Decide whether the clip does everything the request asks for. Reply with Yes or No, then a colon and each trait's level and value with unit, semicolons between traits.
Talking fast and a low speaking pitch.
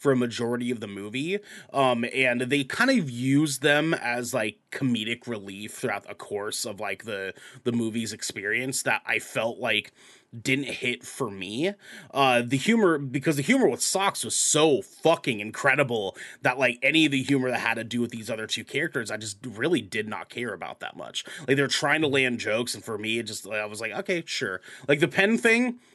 Yes: fast, 210 wpm; low, 130 Hz